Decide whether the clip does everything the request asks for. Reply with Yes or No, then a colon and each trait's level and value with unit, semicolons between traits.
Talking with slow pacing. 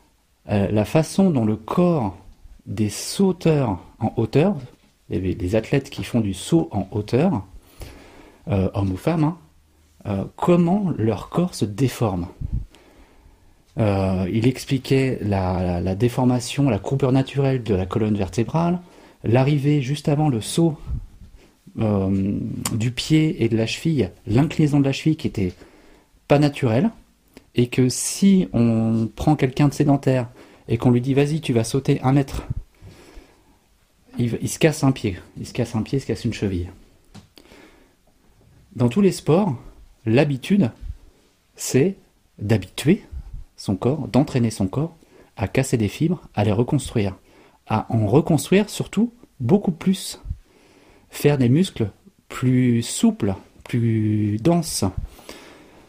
Yes: slow, 135 wpm